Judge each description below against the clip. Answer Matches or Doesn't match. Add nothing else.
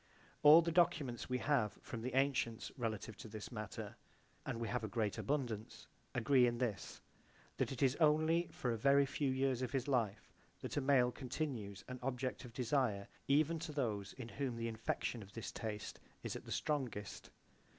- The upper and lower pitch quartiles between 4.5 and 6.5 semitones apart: Doesn't match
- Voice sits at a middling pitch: Doesn't match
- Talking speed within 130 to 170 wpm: Doesn't match